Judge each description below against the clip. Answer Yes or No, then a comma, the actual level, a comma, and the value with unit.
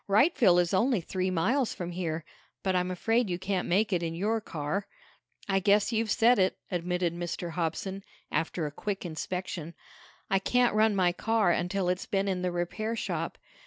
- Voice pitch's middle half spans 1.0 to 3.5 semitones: Yes, average, 3.1 semitones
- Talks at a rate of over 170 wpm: Yes, average, 180 wpm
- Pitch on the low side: No, medium, 185 Hz